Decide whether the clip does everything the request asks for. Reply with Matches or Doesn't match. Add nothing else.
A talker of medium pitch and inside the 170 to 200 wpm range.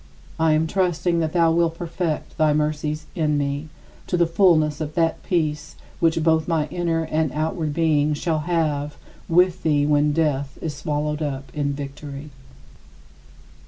Doesn't match